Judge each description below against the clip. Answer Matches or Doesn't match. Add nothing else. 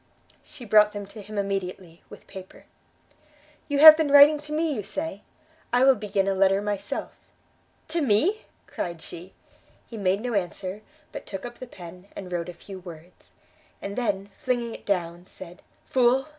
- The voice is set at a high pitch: Matches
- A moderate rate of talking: Matches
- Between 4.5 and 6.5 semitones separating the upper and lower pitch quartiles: Matches